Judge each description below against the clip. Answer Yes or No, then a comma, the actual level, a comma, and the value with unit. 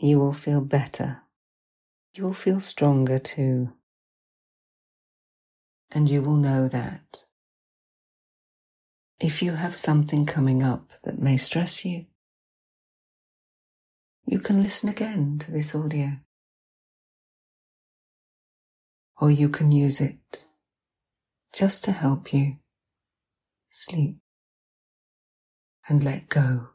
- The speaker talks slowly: Yes, slow, 100 wpm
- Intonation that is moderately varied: Yes, average, 3.4 semitones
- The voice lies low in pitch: No, medium, 150 Hz